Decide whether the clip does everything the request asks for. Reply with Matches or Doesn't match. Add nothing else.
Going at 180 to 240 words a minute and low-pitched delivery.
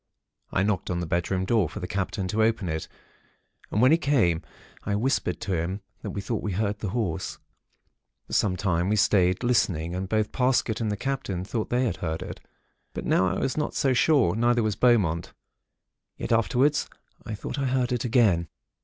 Matches